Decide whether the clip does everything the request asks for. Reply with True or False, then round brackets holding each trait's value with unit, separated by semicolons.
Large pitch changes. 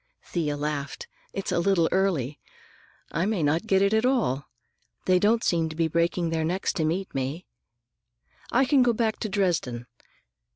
False (4.3 semitones)